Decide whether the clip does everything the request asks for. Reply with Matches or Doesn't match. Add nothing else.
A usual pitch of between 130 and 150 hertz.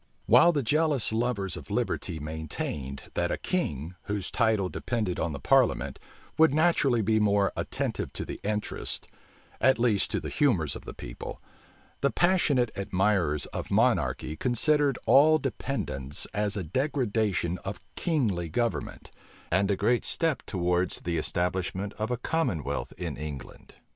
Doesn't match